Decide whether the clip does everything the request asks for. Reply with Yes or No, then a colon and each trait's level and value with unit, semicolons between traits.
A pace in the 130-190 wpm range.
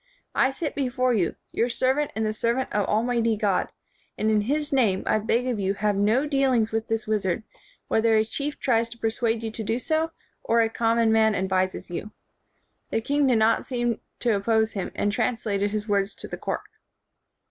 No: fast, 205 wpm